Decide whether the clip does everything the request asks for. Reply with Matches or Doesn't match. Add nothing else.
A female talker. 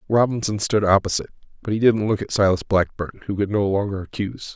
Doesn't match